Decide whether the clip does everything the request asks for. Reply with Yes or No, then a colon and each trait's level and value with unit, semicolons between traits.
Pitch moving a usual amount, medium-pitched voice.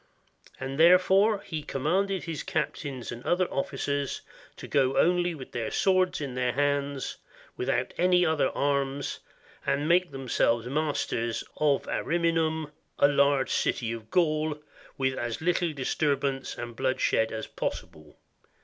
Yes: average, 4.0 semitones; medium, 145 Hz